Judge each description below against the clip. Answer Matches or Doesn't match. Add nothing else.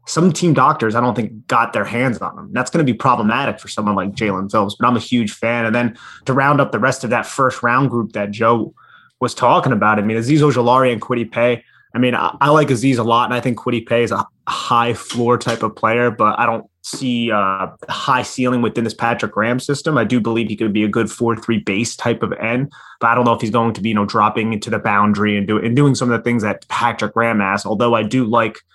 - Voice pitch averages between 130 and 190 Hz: Doesn't match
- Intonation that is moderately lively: Doesn't match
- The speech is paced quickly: Matches